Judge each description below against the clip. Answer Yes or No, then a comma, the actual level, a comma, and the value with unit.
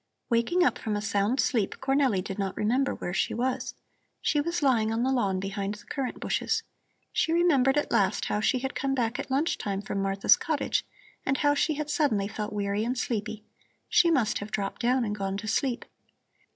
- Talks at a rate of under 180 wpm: No, fast, 205 wpm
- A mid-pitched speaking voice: No, high, 235 Hz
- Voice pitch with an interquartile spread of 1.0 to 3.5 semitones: No, average, 5.0 semitones